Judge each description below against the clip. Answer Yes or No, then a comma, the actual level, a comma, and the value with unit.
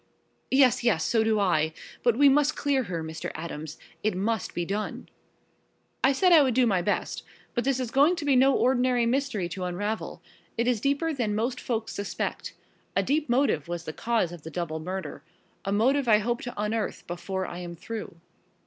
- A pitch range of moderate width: No, wide, 6.3 semitones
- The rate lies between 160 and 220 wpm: Yes, average, 195 wpm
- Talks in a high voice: Yes, high, 225 Hz